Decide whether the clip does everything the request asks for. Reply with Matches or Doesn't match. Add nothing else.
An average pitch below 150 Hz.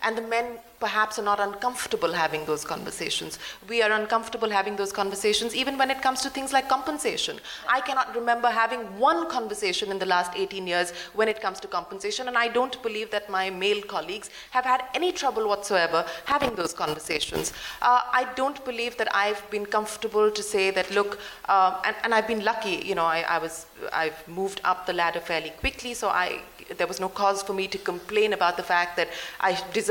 Doesn't match